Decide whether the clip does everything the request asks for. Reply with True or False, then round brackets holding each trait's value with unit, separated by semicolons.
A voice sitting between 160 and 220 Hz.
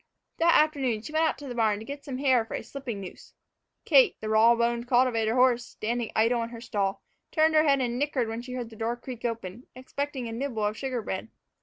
False (240 Hz)